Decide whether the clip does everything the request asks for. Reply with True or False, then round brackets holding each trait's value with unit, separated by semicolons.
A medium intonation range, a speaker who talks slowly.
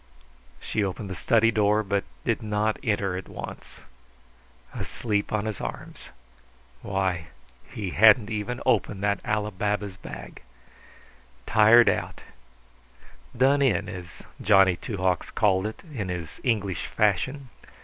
False (2.3 semitones; 130 wpm)